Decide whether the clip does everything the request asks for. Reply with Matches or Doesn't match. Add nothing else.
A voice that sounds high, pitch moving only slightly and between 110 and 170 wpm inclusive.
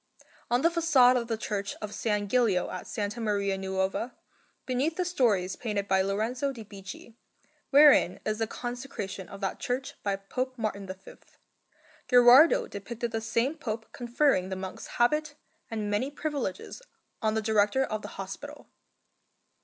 Doesn't match